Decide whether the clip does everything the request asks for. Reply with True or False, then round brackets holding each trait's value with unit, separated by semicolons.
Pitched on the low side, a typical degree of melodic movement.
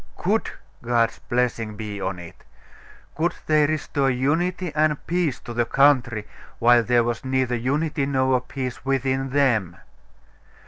True (130 Hz; 3.4 semitones)